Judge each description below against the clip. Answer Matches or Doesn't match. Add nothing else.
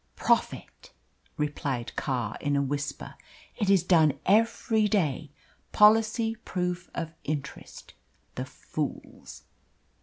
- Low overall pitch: Doesn't match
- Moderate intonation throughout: Doesn't match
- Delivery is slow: Matches